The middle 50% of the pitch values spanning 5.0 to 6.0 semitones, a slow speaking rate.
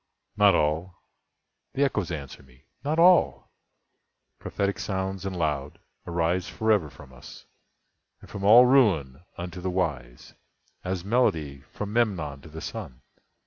Yes: wide, 5.5 semitones; slow, 125 wpm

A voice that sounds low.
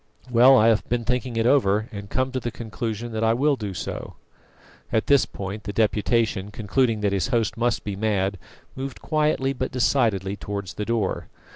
Yes: low, 115 Hz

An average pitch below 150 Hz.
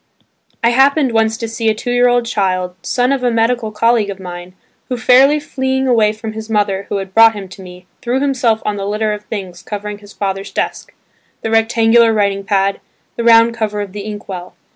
No: high, 220 Hz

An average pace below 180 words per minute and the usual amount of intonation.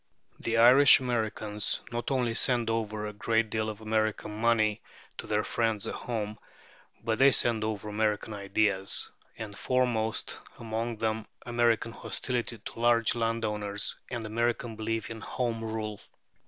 No: average, 140 wpm; narrow, 1.5 semitones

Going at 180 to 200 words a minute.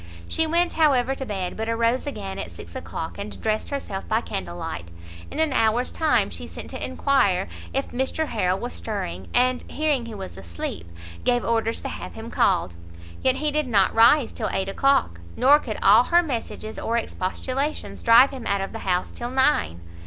Yes: average, 190 wpm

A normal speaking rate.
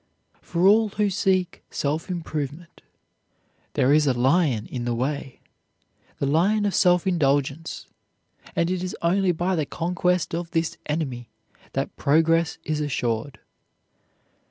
No: slow, 130 wpm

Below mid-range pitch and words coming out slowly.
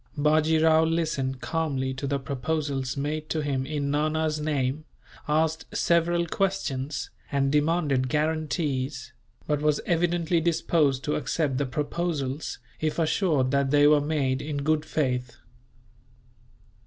No: medium, 150 Hz; slow, 130 wpm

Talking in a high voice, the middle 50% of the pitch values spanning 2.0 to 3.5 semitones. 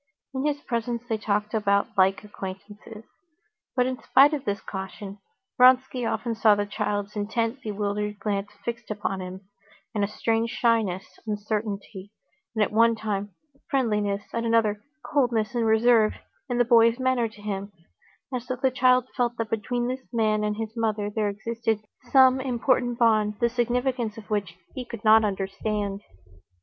Yes: high, 220 Hz; average, 2.7 semitones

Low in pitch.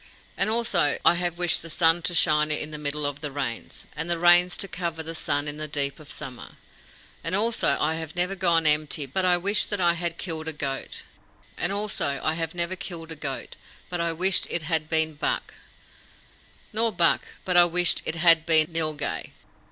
No: medium, 165 Hz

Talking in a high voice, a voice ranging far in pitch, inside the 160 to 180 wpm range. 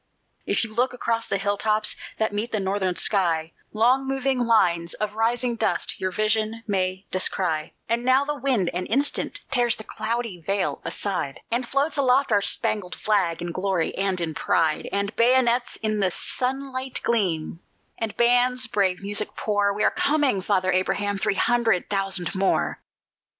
No: high, 215 Hz; average, 4.2 semitones; average, 165 wpm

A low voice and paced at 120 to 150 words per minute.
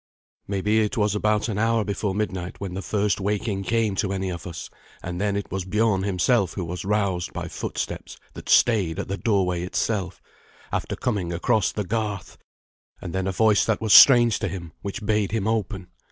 No: low, 100 Hz; average, 195 wpm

